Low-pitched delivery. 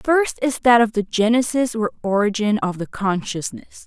No: high, 225 Hz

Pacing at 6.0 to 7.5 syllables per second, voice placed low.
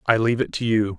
Yes: 6.9 syllables/s; low, 115 Hz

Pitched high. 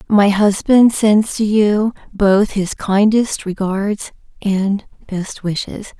Yes: high, 205 Hz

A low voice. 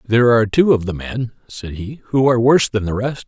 Yes: low, 115 Hz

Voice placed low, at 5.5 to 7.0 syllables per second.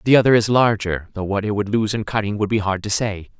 Yes: low, 105 Hz; 6.0 syllables/s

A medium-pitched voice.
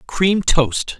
Yes: medium, 160 Hz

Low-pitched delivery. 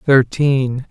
Yes: low, 130 Hz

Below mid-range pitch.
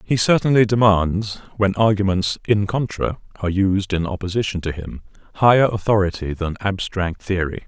Yes: low, 100 Hz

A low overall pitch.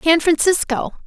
No: very high, 320 Hz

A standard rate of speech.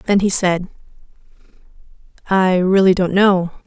No: slow, 115 wpm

